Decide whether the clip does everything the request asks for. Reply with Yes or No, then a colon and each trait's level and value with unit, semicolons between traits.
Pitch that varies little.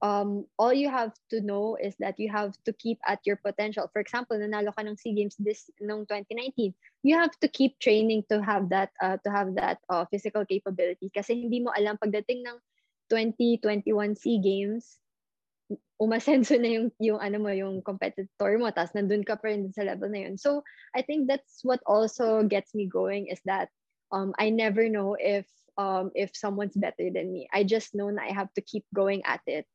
Yes: narrow, 2.2 semitones